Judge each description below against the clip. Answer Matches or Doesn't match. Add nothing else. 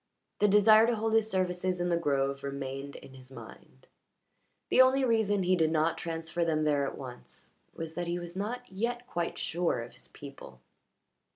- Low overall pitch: Doesn't match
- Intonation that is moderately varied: Doesn't match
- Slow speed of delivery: Doesn't match